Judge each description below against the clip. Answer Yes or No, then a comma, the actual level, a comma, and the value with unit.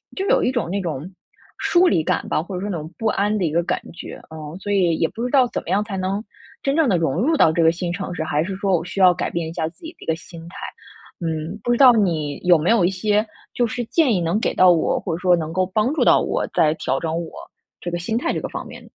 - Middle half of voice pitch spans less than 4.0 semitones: No, average, 4.6 semitones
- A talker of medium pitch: Yes, medium, 180 Hz